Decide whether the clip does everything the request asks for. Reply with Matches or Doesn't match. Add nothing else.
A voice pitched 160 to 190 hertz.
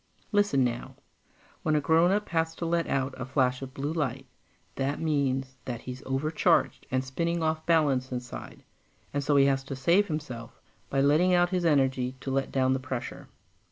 Doesn't match